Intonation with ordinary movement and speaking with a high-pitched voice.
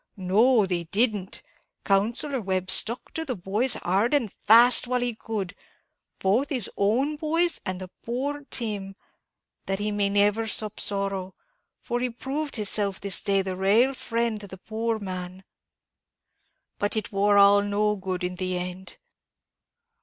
Yes: average, 3.7 semitones; high, 205 Hz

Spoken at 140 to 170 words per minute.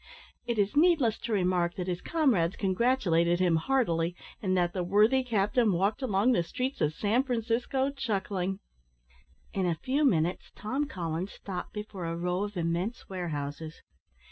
Yes: average, 155 wpm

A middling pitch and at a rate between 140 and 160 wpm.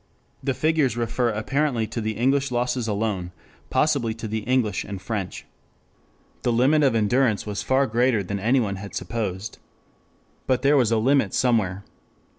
No: low, 115 Hz; average, 155 wpm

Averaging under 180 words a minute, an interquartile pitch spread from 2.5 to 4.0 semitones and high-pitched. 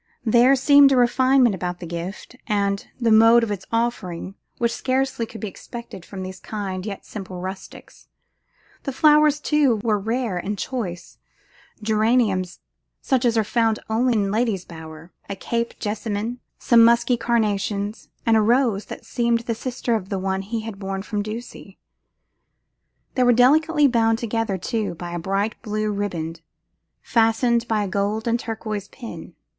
Yes: average, 160 wpm; average, 3.2 semitones; high, 220 Hz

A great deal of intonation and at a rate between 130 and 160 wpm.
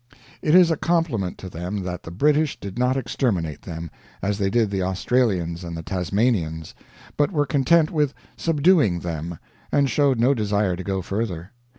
No: wide, 7.9 semitones; average, 175 wpm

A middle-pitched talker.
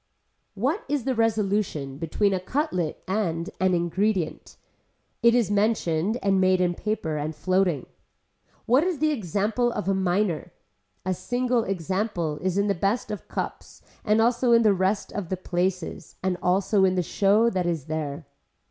No: high, 195 Hz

